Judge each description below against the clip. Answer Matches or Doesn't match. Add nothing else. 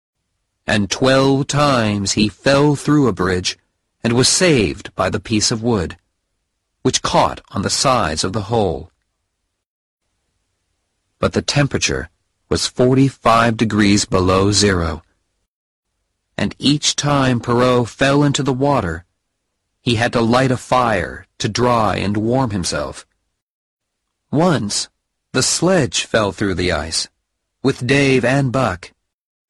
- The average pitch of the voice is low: Matches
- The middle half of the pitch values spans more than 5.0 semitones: Matches